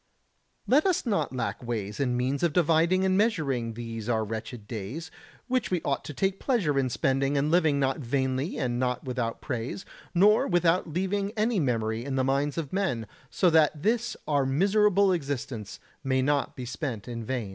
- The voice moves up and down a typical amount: No, wide, 6.7 semitones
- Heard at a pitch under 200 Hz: Yes, medium, 140 Hz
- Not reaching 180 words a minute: No, average, 185 wpm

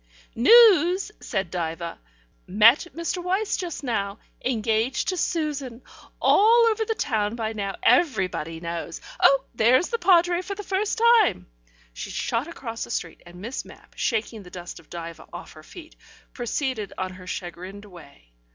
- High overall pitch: Yes, high, 230 Hz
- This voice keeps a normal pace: Yes, average, 155 wpm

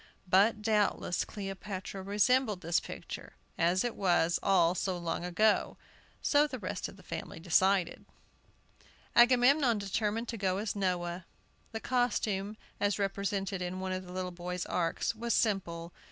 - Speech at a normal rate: Yes, average, 145 wpm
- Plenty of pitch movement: No, average, 3.2 semitones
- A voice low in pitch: No, high, 195 Hz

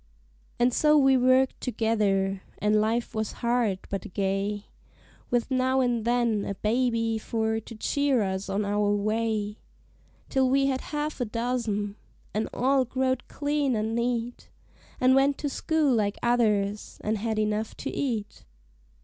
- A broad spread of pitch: No, average, 3.5 semitones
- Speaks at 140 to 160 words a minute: Yes, average, 150 wpm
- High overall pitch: Yes, high, 230 Hz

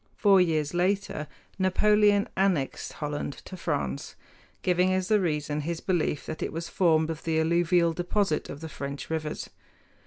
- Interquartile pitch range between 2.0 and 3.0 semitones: No, average, 3.5 semitones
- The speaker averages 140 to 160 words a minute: Yes, average, 150 wpm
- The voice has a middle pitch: Yes, medium, 170 Hz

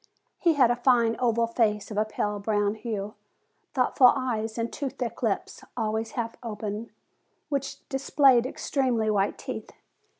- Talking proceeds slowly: No, average, 145 wpm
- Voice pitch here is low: No, high, 230 Hz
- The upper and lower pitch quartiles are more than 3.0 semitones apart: No, average, 2.7 semitones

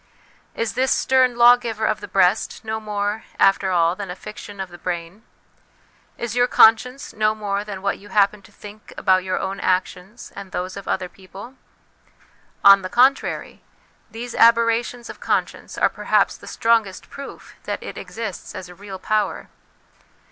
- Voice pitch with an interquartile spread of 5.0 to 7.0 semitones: No, average, 3.3 semitones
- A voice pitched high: Yes, high, 210 Hz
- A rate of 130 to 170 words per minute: Yes, average, 165 wpm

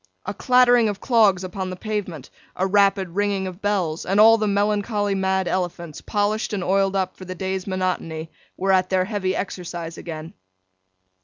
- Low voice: No, high, 190 Hz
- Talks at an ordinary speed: Yes, average, 170 wpm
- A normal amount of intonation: No, narrow, 1.9 semitones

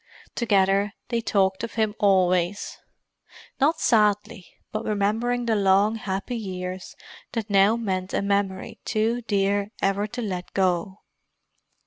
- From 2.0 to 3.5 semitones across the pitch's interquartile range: Yes, narrow, 2.6 semitones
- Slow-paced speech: Yes, slow, 125 wpm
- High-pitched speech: Yes, high, 200 Hz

